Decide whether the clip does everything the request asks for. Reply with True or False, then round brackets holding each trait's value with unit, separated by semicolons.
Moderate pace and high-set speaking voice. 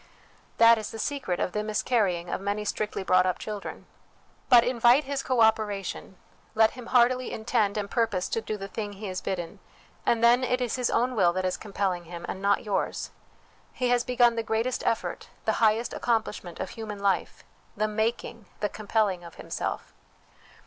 True (190 wpm; 215 Hz)